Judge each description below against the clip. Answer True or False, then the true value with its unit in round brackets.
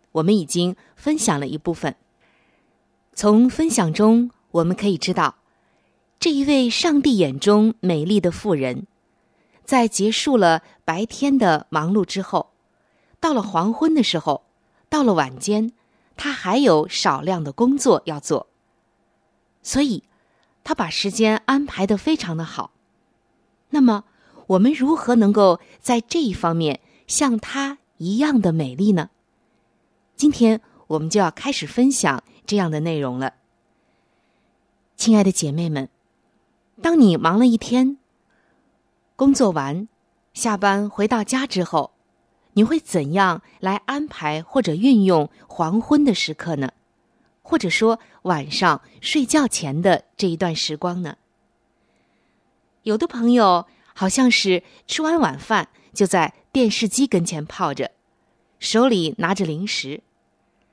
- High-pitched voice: True (210 Hz)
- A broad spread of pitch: True (6.8 semitones)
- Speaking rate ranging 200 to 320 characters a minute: False (190 characters per minute)